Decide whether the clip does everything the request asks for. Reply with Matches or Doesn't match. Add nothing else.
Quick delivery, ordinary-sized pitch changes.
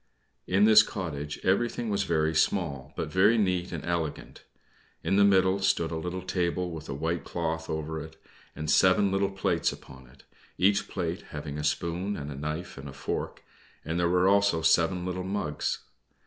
Doesn't match